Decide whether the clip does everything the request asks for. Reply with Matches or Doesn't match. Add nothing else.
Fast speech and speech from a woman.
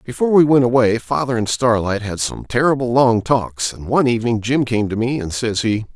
Doesn't match